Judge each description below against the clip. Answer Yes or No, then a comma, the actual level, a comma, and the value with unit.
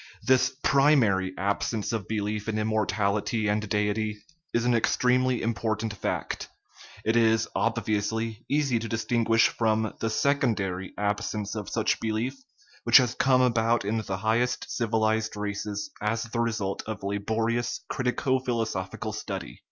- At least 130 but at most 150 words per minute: Yes, slow, 135 wpm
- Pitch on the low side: Yes, low, 110 Hz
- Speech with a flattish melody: Yes, narrow, 2.0 semitones